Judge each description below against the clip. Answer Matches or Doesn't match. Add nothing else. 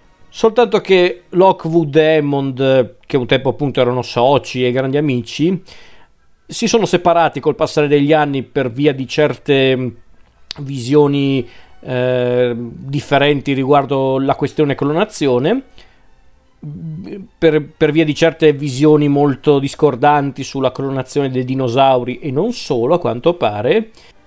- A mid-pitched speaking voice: Matches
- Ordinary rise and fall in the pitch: Matches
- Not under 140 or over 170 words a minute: Doesn't match